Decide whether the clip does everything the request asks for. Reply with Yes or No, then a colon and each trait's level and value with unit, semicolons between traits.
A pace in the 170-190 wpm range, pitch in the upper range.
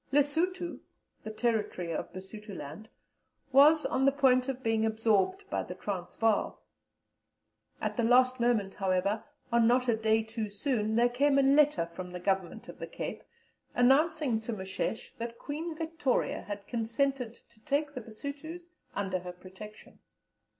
No: average, 150 wpm; high, 235 Hz